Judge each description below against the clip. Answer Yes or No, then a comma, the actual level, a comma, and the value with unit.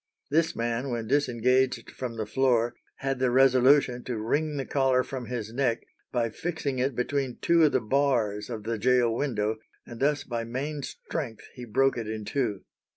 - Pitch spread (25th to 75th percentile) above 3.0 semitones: No, average, 2.7 semitones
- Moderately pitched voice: No, low, 125 Hz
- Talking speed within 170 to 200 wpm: Yes, average, 180 wpm